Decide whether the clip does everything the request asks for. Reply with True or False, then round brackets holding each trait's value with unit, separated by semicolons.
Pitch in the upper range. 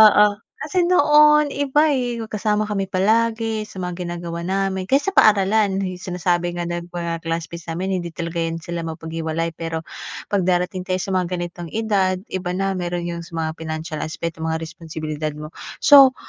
False (180 Hz)